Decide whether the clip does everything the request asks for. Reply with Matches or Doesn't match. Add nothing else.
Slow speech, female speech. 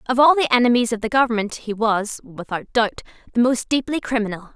Doesn't match